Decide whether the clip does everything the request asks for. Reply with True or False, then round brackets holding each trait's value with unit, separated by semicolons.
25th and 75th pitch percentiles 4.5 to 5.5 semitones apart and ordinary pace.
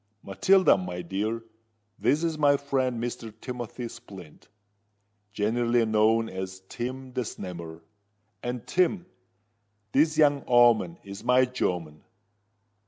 False (4.9 semitones; 110 wpm)